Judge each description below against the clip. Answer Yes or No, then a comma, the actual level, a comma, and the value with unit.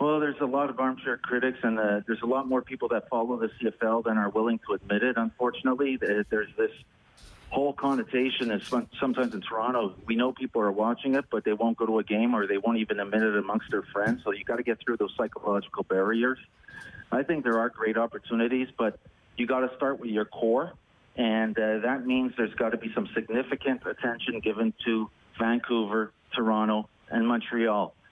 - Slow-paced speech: No, fast, 205 wpm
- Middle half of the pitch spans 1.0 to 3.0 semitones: Yes, narrow, 2.6 semitones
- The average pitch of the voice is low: Yes, low, 115 Hz